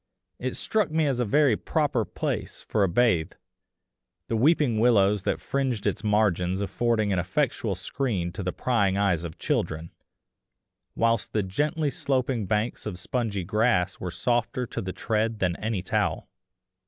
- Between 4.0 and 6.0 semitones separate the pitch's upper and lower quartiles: Yes, average, 4.7 semitones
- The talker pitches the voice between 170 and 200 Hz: No, low, 110 Hz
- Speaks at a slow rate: No, average, 155 wpm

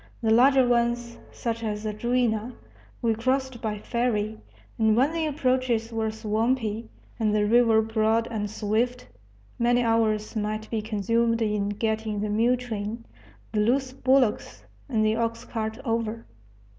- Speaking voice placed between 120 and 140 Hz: No, high, 225 Hz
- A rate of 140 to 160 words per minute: Yes, average, 145 wpm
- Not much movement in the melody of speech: Yes, narrow, 2.0 semitones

